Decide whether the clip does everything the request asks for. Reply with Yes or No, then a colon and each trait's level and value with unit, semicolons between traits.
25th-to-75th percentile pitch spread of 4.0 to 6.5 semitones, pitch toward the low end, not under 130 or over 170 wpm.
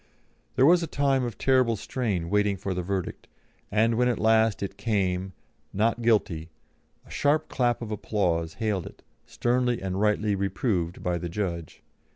Yes: average, 4.4 semitones; low, 105 Hz; average, 165 wpm